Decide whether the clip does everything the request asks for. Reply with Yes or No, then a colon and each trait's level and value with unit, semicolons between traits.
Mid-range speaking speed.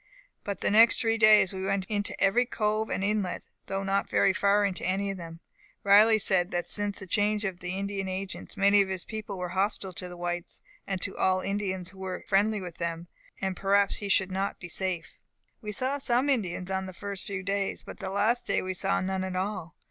No: fast, 220 wpm